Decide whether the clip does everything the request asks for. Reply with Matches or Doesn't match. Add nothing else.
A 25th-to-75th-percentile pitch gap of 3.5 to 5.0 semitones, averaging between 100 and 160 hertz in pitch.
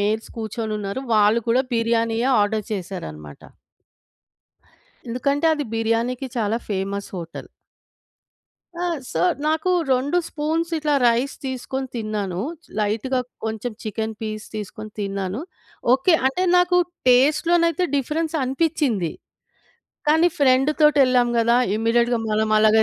Doesn't match